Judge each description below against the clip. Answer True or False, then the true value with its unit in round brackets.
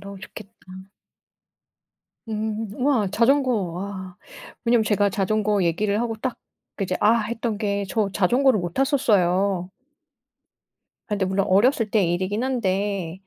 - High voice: True (205 Hz)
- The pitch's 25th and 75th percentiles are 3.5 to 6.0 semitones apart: False (3.1 semitones)